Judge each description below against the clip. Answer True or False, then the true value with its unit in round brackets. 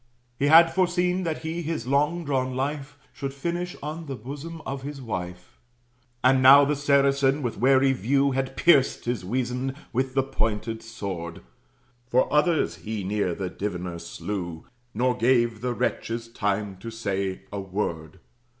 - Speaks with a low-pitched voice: True (130 Hz)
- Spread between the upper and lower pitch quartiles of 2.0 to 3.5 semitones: False (5.1 semitones)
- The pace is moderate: True (155 wpm)